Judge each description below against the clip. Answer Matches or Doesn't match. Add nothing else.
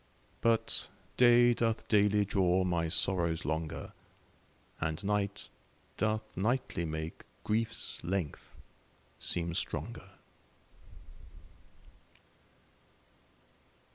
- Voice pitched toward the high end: Doesn't match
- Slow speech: Matches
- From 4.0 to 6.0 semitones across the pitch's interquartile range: Matches